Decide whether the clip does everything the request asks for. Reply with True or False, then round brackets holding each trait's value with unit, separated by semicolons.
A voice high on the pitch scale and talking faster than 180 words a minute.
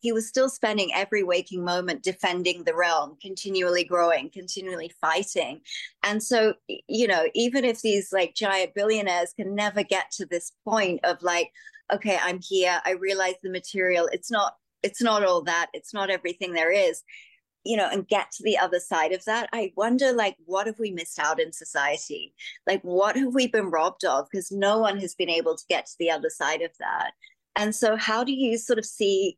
True (195 Hz; 200 wpm)